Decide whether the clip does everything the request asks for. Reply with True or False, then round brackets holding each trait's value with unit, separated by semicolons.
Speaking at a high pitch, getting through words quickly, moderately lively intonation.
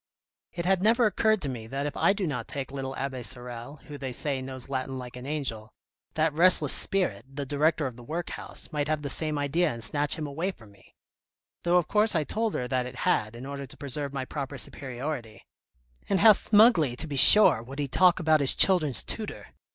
False (140 Hz; 220 wpm; 4.6 semitones)